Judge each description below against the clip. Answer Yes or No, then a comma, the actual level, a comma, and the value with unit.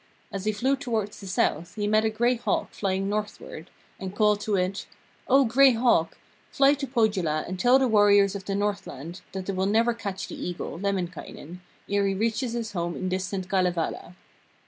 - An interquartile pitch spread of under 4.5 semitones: Yes, average, 3.2 semitones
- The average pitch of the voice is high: Yes, high, 200 Hz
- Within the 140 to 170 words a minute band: No, average, 190 wpm